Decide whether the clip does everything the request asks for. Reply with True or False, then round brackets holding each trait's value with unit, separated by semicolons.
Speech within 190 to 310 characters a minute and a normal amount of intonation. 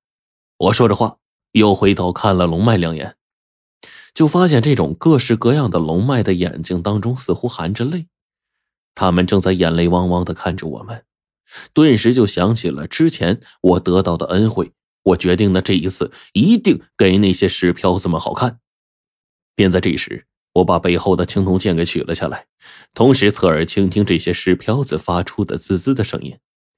True (260 characters per minute; 4.7 semitones)